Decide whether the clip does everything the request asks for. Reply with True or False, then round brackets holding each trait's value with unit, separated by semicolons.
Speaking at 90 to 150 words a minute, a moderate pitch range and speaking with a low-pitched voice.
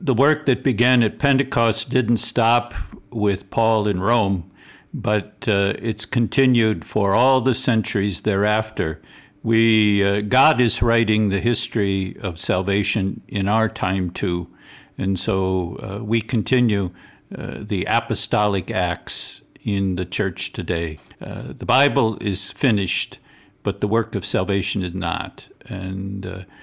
True (135 wpm; 3.2 semitones; 105 Hz)